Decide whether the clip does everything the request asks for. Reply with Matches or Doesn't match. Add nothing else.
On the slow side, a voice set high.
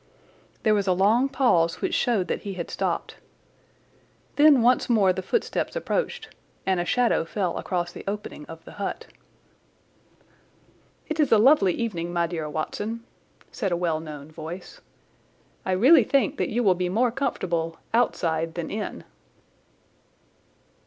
Doesn't match